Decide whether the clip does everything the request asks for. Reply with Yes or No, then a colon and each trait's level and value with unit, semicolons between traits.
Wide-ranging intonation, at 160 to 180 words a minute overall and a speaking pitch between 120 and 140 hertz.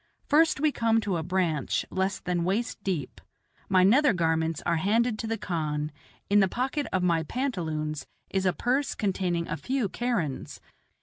No: wide, 6.0 semitones; average, 170 wpm; high, 190 Hz